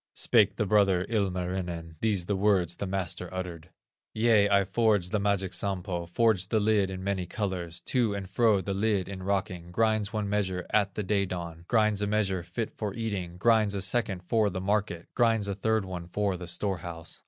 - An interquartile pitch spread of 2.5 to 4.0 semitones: Yes, average, 2.8 semitones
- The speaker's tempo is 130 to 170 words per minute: No, average, 195 wpm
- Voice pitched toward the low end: Yes, low, 100 Hz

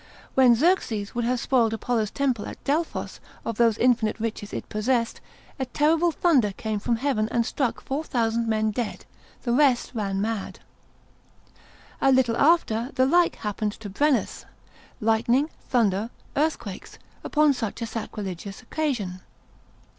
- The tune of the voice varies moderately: Yes, average, 3.9 semitones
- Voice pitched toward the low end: No, high, 235 Hz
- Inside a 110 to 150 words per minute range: Yes, average, 140 wpm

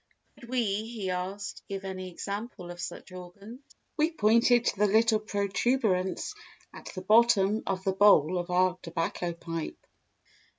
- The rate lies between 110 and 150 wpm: Yes, average, 145 wpm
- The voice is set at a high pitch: Yes, high, 195 Hz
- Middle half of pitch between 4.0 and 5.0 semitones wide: No, average, 3.4 semitones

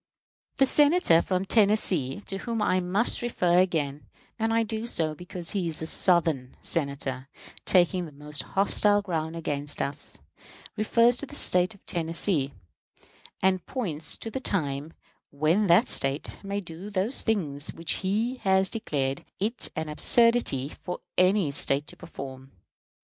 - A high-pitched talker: No, medium, 180 Hz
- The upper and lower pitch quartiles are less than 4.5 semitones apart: No, wide, 5.6 semitones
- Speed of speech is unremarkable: Yes, average, 150 wpm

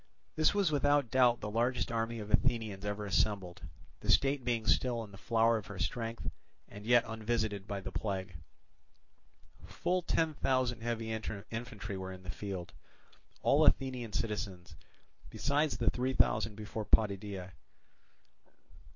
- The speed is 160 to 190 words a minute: No, average, 140 wpm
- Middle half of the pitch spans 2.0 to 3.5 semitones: Yes, average, 3.2 semitones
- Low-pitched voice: Yes, low, 110 Hz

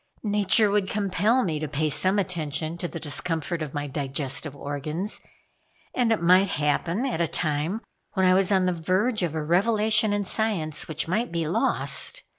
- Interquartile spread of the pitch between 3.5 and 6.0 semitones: Yes, average, 4.8 semitones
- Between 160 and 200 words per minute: Yes, average, 180 wpm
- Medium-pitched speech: Yes, medium, 175 Hz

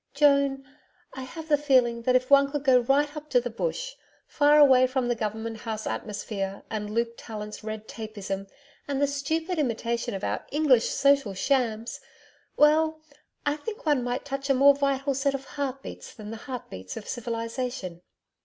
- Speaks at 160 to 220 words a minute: Yes, average, 180 wpm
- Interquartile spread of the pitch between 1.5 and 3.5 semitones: No, average, 3.9 semitones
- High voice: Yes, very high, 260 Hz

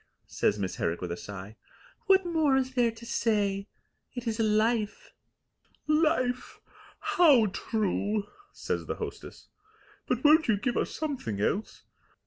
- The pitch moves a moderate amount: No, wide, 6.4 semitones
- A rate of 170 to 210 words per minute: No, slow, 135 wpm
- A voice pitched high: Yes, high, 230 Hz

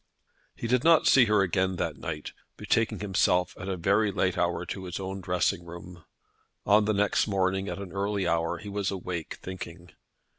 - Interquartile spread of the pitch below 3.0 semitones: Yes, narrow, 2.4 semitones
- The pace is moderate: Yes, average, 185 wpm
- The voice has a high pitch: No, very low, 95 Hz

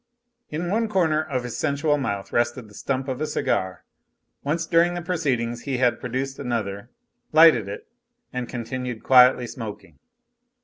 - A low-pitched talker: Yes, low, 130 Hz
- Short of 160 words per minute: Yes, average, 150 wpm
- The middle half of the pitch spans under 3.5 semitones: No, average, 4.6 semitones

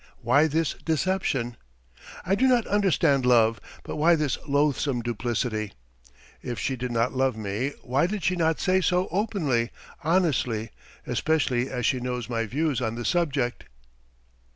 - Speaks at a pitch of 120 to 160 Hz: Yes, low, 135 Hz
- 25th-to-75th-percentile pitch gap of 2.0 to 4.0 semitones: No, wide, 5.4 semitones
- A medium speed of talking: Yes, average, 150 wpm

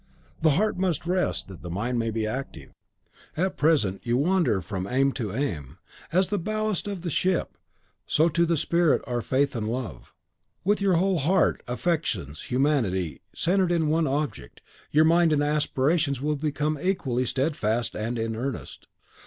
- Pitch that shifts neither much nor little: No, wide, 6.4 semitones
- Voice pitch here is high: No, medium, 145 Hz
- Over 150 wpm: Yes, average, 165 wpm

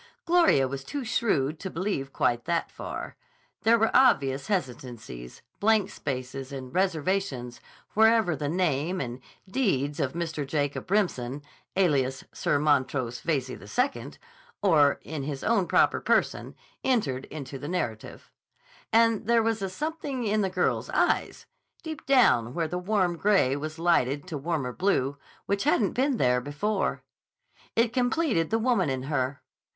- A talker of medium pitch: Yes, medium, 165 Hz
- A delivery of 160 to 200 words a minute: No, average, 145 wpm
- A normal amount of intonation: No, wide, 7.6 semitones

